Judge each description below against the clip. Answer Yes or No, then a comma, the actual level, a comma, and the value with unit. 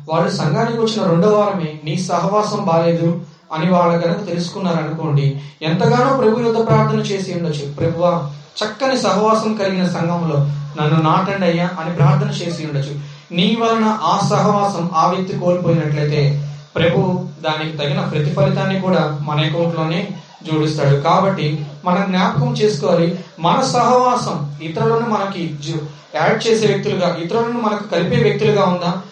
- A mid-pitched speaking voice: Yes, medium, 170 Hz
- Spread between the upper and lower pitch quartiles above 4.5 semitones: No, average, 4.1 semitones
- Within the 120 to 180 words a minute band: Yes, fast, 125 wpm